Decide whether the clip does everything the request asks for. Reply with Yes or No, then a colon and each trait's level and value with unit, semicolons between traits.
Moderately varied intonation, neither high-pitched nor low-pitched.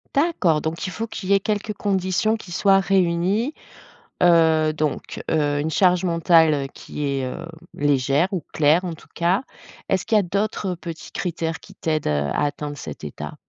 Yes: average, 3.9 semitones; medium, 170 Hz